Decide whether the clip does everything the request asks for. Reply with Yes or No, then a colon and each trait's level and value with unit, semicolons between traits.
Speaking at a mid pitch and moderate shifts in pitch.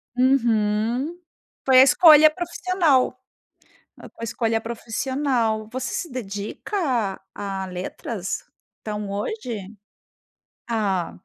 No: high, 235 Hz; average, 4.6 semitones